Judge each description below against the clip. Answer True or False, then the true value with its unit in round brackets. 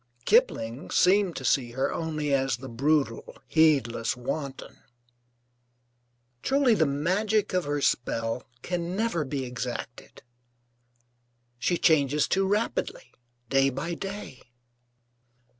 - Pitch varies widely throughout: True (5.8 semitones)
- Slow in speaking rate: True (110 wpm)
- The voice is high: False (150 Hz)